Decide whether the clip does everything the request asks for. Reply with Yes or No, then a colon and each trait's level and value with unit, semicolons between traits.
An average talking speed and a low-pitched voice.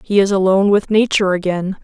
No: average, 195 wpm; high, 195 Hz